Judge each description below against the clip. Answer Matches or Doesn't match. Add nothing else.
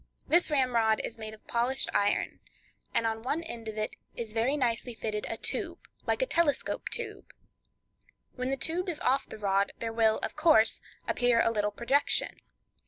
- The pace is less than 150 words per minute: Doesn't match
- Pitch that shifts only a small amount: Doesn't match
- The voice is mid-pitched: Doesn't match